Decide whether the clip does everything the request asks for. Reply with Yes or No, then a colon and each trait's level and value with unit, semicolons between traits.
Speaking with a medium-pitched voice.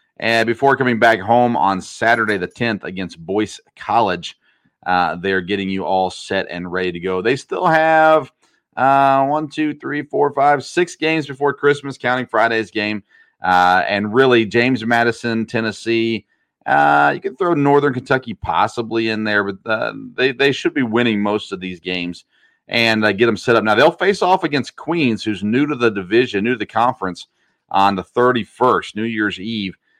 No: low, 115 Hz